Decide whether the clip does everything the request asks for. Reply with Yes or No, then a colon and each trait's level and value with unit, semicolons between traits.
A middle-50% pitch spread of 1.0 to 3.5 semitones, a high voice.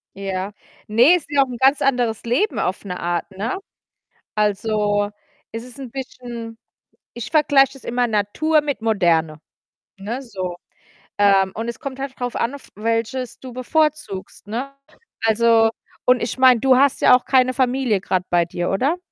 No: average, 4.3 semitones; high, 235 Hz